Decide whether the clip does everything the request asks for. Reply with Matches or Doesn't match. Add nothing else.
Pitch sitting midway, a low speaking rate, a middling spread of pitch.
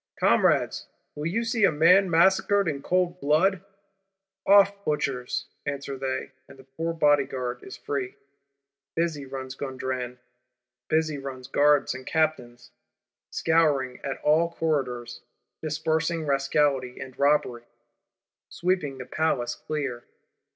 Matches